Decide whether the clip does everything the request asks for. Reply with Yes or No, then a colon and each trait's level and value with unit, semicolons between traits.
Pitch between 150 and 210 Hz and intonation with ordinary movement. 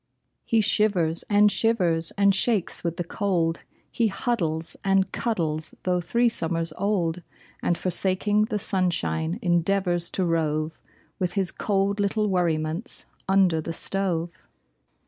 Yes: medium, 185 Hz; average, 3.3 semitones